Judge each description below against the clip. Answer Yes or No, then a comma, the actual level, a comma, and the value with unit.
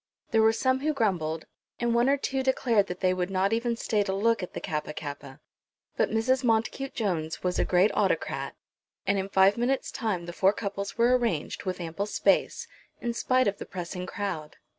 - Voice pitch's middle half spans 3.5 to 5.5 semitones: Yes, average, 4.6 semitones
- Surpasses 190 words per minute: Yes, average, 200 wpm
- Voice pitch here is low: No, high, 200 Hz